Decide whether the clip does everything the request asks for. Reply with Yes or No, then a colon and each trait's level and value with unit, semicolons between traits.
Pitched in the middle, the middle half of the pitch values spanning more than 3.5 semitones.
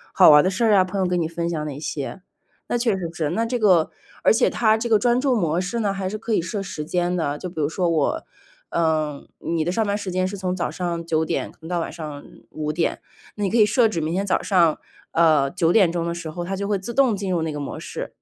Yes: medium, 180 Hz; average, 3.9 semitones